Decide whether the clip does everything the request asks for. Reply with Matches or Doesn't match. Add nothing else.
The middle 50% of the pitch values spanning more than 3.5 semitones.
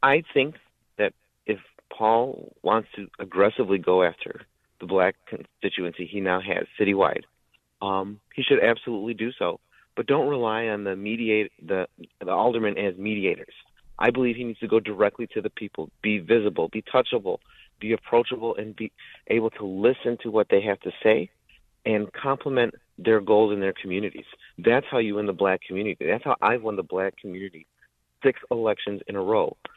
Doesn't match